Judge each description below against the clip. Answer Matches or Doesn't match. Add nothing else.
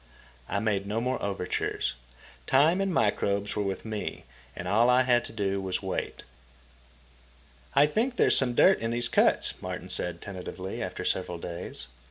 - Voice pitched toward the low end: Matches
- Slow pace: Doesn't match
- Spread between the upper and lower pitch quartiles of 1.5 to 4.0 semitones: Doesn't match